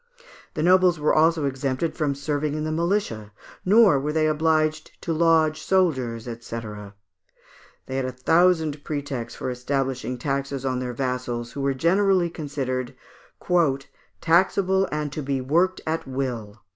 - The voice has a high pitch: No, medium, 145 Hz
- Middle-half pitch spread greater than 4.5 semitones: No, average, 4.0 semitones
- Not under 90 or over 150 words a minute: Yes, average, 145 wpm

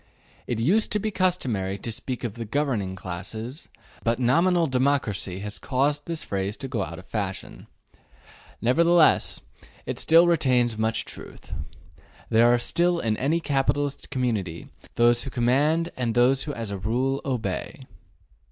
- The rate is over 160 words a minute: No, average, 150 wpm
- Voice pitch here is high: No, low, 125 Hz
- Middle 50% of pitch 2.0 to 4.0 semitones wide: No, average, 4.9 semitones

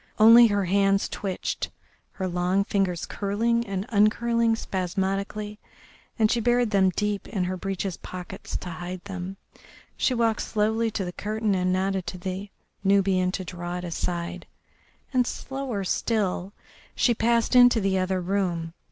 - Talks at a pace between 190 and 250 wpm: No, average, 150 wpm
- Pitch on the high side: Yes, high, 195 Hz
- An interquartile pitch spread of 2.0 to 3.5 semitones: Yes, average, 3.1 semitones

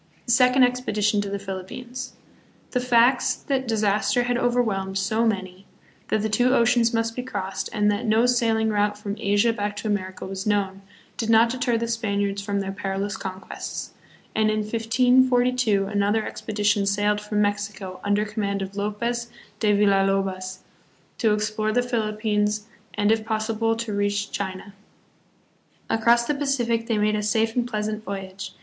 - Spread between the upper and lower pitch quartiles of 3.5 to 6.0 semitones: No, narrow, 2.5 semitones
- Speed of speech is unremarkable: Yes, average, 160 wpm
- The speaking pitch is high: Yes, high, 215 Hz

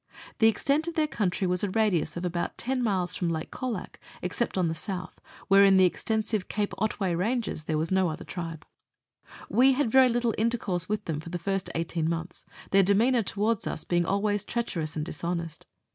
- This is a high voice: Yes, high, 195 Hz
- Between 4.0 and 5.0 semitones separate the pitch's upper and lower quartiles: Yes, average, 4.4 semitones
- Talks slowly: No, average, 195 wpm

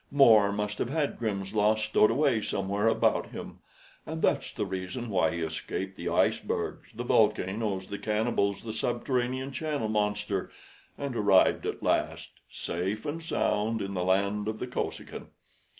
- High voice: No, low, 105 Hz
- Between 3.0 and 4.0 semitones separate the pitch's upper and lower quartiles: Yes, average, 3.3 semitones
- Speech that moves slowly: No, average, 155 wpm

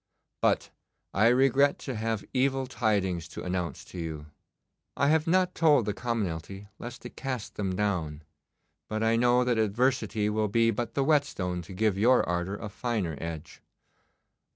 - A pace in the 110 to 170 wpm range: Yes, average, 160 wpm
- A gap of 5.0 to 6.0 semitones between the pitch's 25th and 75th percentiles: Yes, average, 5.3 semitones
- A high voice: No, low, 110 Hz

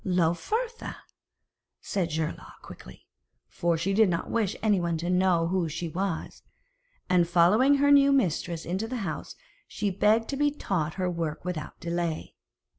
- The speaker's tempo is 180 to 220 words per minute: No, average, 150 wpm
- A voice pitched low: No, medium, 180 Hz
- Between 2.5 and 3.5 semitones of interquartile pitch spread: No, average, 4.5 semitones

